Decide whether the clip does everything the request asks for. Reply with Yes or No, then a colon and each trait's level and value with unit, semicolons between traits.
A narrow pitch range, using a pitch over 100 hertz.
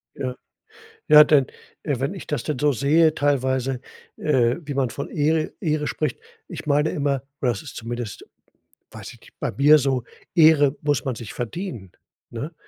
No: average, 3.0 semitones; medium, 140 Hz